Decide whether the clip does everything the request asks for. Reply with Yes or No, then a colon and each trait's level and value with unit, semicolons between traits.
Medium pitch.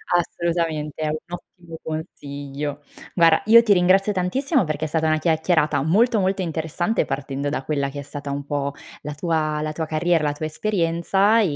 Yes: medium, 160 Hz